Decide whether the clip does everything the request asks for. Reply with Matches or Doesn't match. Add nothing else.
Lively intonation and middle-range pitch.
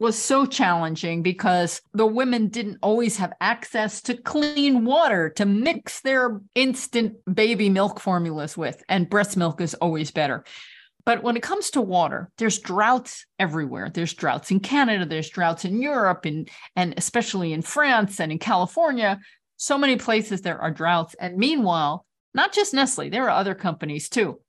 Doesn't match